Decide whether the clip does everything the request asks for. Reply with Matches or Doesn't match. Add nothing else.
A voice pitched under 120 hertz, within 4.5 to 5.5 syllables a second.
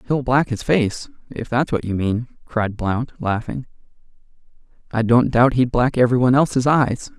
Doesn't match